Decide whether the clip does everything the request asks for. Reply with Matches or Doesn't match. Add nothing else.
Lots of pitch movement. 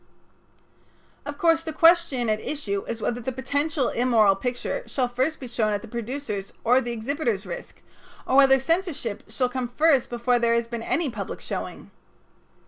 Doesn't match